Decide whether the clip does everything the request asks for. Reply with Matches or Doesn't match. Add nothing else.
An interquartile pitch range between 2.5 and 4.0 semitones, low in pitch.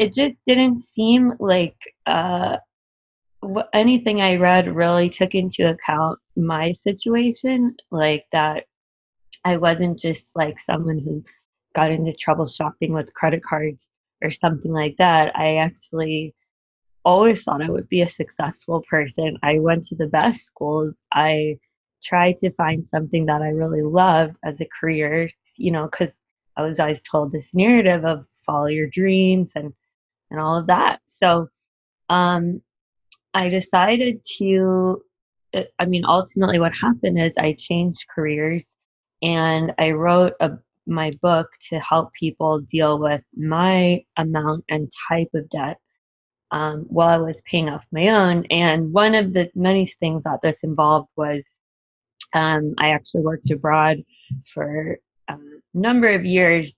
Doesn't match